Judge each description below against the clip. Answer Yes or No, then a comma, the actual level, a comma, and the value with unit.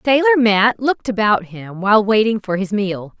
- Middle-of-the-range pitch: No, high, 215 Hz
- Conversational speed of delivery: Yes, average, 190 wpm